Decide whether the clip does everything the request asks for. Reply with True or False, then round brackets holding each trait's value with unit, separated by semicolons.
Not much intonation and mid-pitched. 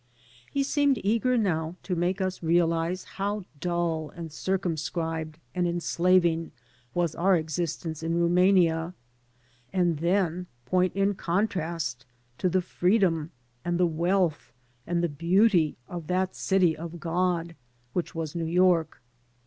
True (2.1 semitones; 175 Hz)